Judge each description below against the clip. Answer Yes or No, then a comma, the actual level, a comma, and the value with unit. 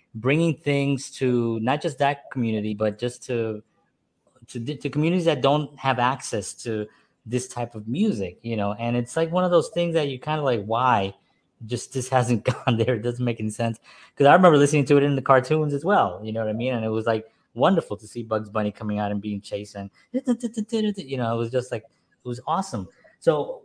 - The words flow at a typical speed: No, fast, 225 wpm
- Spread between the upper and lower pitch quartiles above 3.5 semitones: Yes, average, 4.6 semitones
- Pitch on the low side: Yes, low, 125 Hz